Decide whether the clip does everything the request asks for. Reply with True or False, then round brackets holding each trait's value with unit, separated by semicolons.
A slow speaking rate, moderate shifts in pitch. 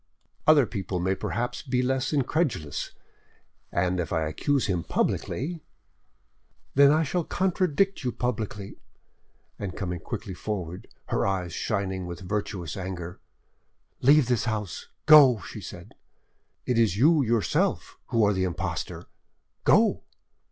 False (125 wpm; 6.6 semitones)